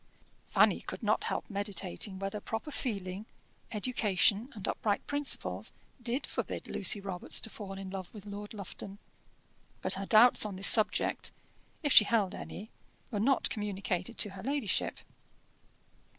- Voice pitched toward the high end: Yes, high, 205 Hz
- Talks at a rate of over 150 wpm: No, average, 145 wpm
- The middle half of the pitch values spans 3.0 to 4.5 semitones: No, narrow, 2.5 semitones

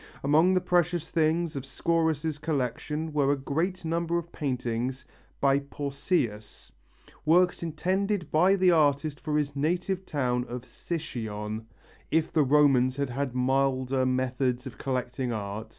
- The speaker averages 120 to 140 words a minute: Yes, slow, 135 wpm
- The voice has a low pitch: No, medium, 145 Hz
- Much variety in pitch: No, average, 4.3 semitones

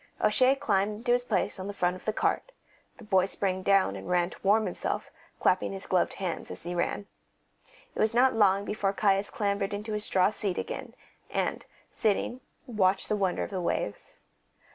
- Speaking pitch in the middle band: No, high, 200 Hz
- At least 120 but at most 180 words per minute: No, average, 190 wpm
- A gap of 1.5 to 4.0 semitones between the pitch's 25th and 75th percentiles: Yes, narrow, 2.4 semitones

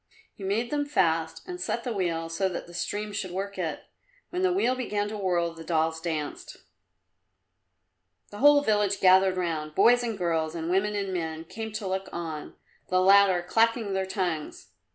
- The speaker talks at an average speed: Yes, average, 180 wpm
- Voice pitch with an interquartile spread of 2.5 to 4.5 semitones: Yes, average, 4.1 semitones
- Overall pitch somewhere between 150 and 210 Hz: Yes, high, 190 Hz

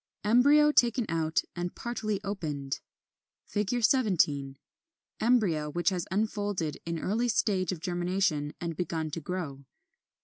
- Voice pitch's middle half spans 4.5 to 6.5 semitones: Yes, average, 5.2 semitones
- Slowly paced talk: Yes, slow, 115 wpm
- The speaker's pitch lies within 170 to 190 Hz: Yes, medium, 185 Hz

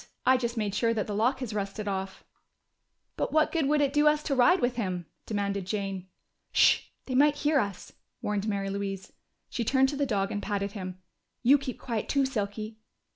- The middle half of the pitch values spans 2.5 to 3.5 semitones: No, average, 5.1 semitones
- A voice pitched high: Yes, high, 220 Hz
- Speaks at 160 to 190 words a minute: No, average, 200 wpm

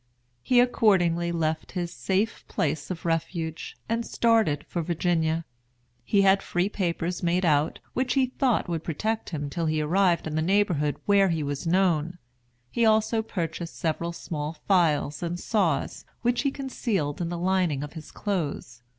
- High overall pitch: No, medium, 175 Hz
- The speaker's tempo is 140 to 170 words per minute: Yes, average, 160 wpm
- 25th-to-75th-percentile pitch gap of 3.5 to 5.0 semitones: Yes, average, 4.0 semitones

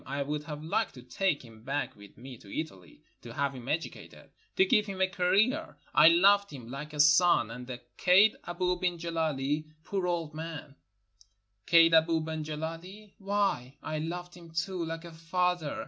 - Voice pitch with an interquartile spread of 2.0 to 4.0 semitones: Yes, average, 3.7 semitones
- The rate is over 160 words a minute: Yes, average, 180 wpm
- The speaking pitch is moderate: Yes, medium, 165 Hz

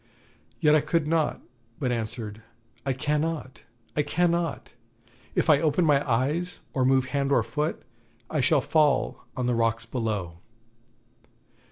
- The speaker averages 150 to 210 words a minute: No, average, 140 wpm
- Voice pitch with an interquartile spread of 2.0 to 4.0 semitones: No, average, 4.4 semitones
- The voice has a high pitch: No, medium, 140 Hz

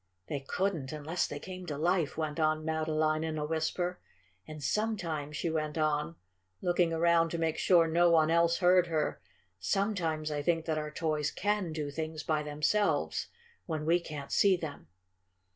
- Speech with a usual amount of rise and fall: No, narrow, 2.1 semitones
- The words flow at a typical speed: Yes, average, 170 wpm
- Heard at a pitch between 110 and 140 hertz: No, medium, 160 Hz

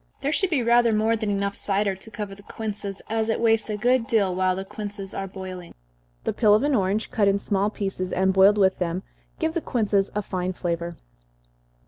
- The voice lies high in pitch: Yes, high, 205 Hz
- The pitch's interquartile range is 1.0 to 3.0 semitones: Yes, average, 2.7 semitones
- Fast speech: Yes, fast, 210 wpm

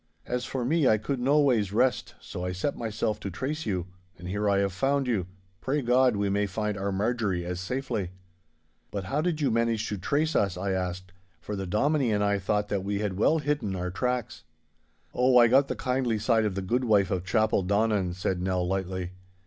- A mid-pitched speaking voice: No, low, 105 Hz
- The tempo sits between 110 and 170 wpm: No, fast, 205 wpm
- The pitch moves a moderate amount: Yes, average, 4.8 semitones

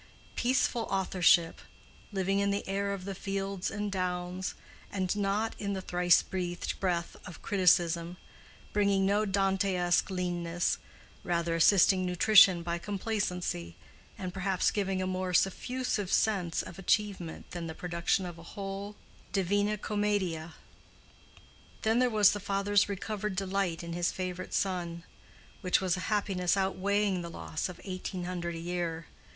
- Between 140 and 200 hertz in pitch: Yes, medium, 185 Hz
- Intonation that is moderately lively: No, narrow, 2.3 semitones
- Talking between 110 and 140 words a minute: Yes, slow, 135 wpm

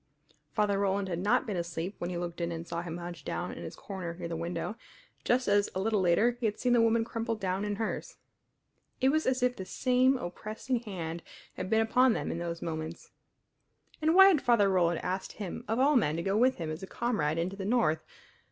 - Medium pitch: No, high, 195 Hz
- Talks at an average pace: No, fast, 225 wpm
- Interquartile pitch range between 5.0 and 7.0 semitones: Yes, average, 5.3 semitones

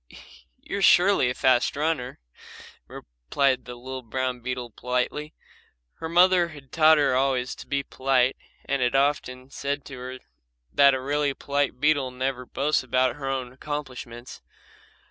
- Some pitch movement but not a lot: No, narrow, 2.3 semitones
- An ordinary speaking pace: Yes, average, 150 wpm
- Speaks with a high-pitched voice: No, low, 135 Hz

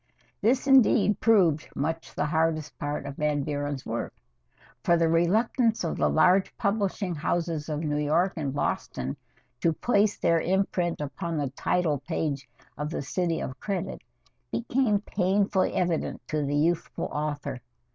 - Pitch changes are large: No, average, 4.5 semitones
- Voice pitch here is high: No, medium, 165 Hz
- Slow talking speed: No, average, 145 wpm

